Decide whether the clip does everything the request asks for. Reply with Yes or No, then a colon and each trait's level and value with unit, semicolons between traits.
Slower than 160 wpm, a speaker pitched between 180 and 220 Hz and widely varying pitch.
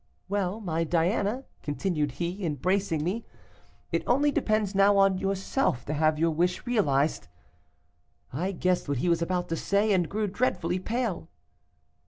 No: average, 150 wpm; medium, 185 Hz; average, 3.7 semitones